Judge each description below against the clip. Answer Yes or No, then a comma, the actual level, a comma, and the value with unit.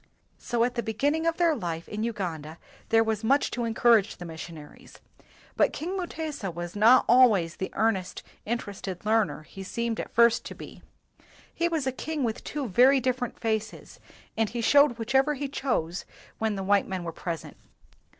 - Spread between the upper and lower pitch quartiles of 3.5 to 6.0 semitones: Yes, average, 5.2 semitones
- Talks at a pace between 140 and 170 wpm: No, average, 180 wpm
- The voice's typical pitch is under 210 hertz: No, high, 225 Hz